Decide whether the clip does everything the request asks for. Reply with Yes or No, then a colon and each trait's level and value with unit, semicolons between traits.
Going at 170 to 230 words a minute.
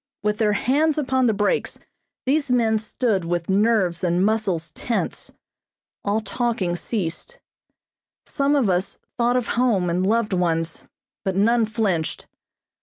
No: slow, 135 wpm